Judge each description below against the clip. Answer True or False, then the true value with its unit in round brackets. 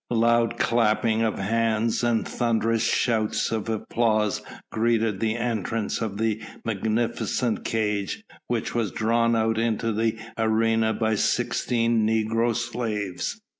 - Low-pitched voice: True (115 Hz)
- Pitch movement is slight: True (1.1 semitones)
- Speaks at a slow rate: True (120 wpm)